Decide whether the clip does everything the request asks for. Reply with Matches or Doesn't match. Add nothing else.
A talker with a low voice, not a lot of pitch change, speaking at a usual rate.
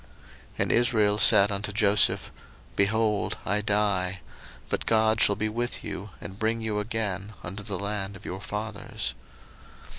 Matches